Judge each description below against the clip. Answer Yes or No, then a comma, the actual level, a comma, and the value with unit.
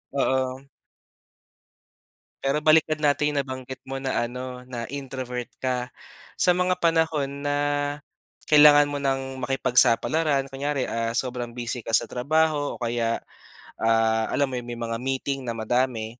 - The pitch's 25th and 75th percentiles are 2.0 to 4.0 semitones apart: Yes, average, 2.8 semitones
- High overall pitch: No, low, 130 Hz